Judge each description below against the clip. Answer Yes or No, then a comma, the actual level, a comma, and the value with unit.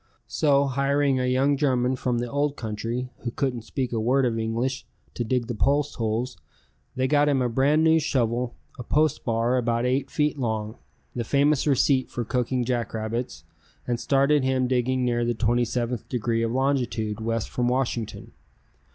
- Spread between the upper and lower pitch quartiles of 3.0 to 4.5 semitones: No, narrow, 2.6 semitones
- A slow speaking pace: No, average, 170 wpm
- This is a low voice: Yes, low, 125 Hz